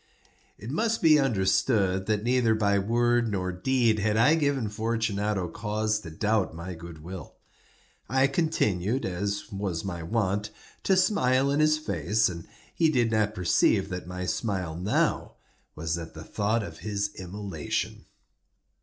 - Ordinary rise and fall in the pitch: Yes, average, 4.4 semitones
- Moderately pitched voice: No, low, 105 Hz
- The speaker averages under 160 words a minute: Yes, average, 150 wpm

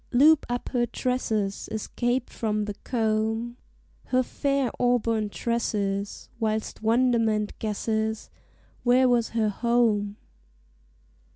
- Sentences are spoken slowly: Yes, slow, 100 wpm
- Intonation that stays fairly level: Yes, narrow, 2.3 semitones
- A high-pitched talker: Yes, high, 225 Hz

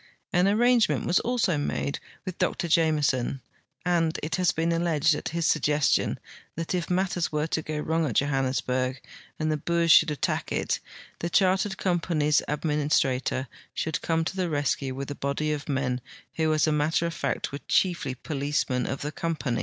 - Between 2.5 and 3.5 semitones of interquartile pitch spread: Yes, average, 3.1 semitones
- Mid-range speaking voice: Yes, medium, 155 Hz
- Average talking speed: Yes, average, 175 wpm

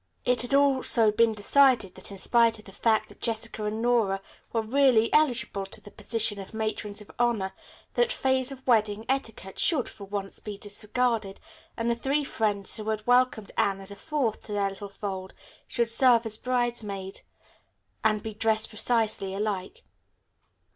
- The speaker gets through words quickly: No, average, 170 wpm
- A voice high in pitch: Yes, high, 220 Hz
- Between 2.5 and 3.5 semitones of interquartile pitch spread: Yes, average, 3.1 semitones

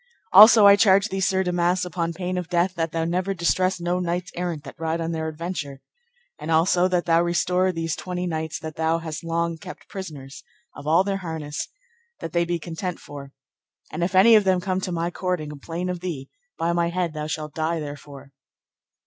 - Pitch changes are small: Yes, narrow, 2.3 semitones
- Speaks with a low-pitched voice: No, medium, 170 Hz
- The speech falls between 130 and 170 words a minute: No, fast, 205 wpm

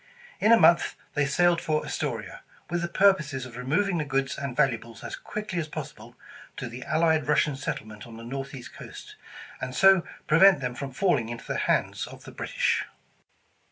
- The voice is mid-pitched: Yes, medium, 145 Hz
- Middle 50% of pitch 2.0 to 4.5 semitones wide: No, average, 5.3 semitones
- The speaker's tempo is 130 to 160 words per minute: No, average, 180 wpm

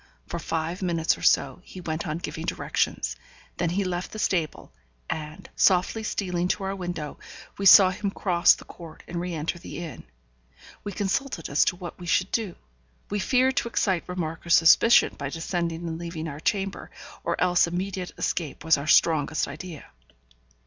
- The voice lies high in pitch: No, medium, 175 Hz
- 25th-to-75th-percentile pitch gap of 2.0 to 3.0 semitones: Yes, narrow, 2.6 semitones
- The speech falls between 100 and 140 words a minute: No, average, 175 wpm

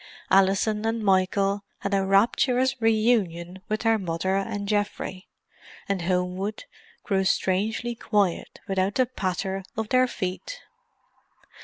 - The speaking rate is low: Yes, slow, 120 wpm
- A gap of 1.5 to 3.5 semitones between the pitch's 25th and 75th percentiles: Yes, average, 2.8 semitones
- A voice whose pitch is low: No, high, 200 Hz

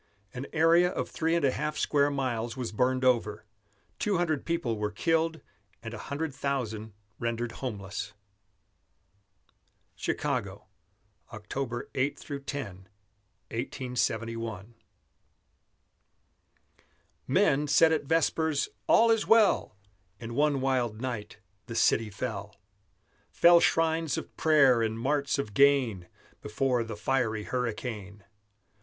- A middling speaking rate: No, slow, 110 wpm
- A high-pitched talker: No, low, 125 Hz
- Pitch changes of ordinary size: Yes, average, 4.7 semitones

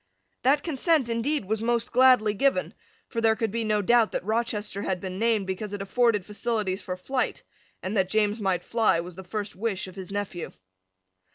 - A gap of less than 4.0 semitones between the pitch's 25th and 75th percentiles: Yes, average, 3.4 semitones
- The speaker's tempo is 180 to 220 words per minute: Yes, average, 190 wpm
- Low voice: No, high, 215 Hz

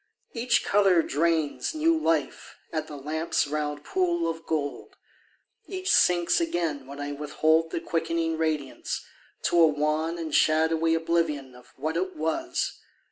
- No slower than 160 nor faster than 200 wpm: No, average, 140 wpm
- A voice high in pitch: No, medium, 160 Hz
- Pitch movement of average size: No, narrow, 2.2 semitones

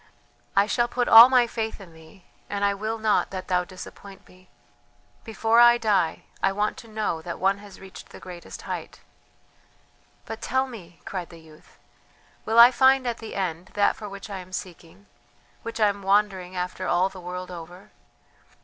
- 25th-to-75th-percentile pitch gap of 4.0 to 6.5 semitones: No, average, 3.6 semitones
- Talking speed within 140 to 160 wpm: No, average, 185 wpm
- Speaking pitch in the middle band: No, high, 195 Hz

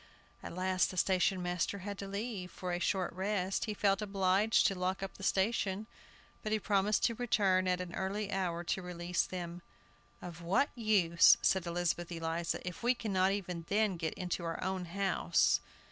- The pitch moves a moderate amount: No, narrow, 2.2 semitones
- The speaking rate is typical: Yes, average, 180 wpm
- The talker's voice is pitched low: No, medium, 185 Hz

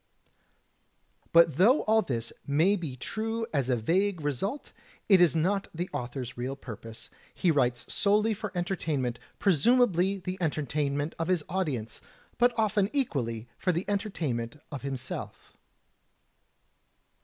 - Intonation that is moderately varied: No, wide, 7.1 semitones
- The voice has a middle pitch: Yes, medium, 165 Hz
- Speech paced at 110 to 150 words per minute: Yes, slow, 135 wpm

